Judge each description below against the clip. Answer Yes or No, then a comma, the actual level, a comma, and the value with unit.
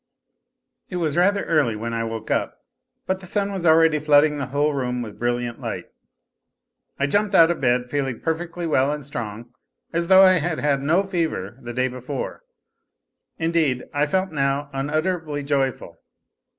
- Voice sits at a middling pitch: Yes, medium, 145 Hz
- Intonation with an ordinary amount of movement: Yes, average, 4.8 semitones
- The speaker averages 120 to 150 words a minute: No, average, 165 wpm